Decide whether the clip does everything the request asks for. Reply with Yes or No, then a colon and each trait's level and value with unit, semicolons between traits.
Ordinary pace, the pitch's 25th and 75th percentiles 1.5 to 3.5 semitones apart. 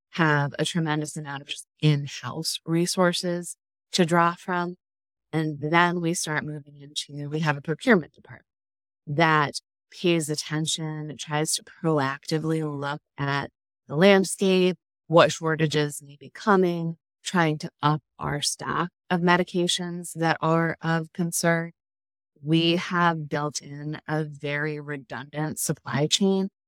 No: slow, 125 wpm; narrow, 2.5 semitones